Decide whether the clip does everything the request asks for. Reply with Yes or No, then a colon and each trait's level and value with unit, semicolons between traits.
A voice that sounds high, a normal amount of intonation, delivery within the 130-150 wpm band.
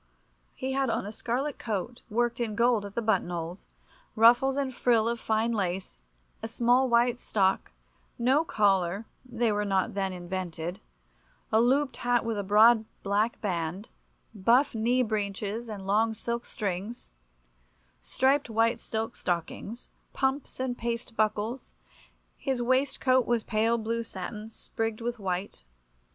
Yes: high, 225 Hz; average, 3.1 semitones; average, 140 wpm